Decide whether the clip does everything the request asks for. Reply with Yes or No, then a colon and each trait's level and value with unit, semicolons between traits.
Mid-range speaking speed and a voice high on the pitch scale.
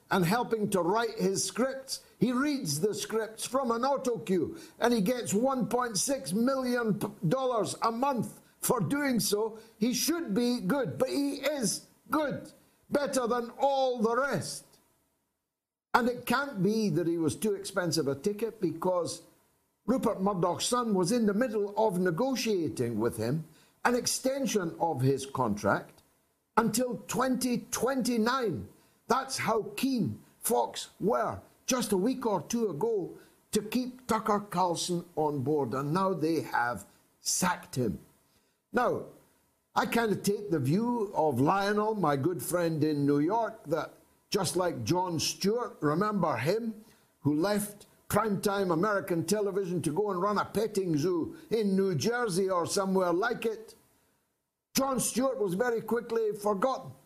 Yes: average, 145 wpm; high, 210 Hz